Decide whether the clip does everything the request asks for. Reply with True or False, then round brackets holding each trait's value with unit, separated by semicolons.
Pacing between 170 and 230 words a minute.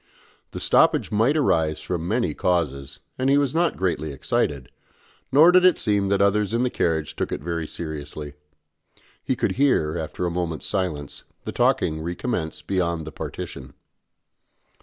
False (160 wpm)